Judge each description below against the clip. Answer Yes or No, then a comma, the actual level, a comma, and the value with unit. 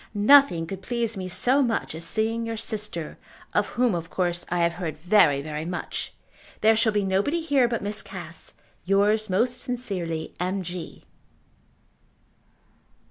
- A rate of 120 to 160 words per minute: Yes, average, 150 wpm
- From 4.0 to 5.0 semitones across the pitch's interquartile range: Yes, average, 4.7 semitones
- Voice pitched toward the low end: No, high, 195 Hz